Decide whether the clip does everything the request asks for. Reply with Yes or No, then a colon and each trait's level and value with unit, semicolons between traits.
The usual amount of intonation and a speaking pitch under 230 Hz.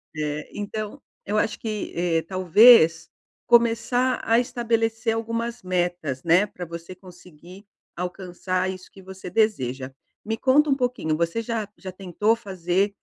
Yes: average, 4.4 semitones; high, 190 Hz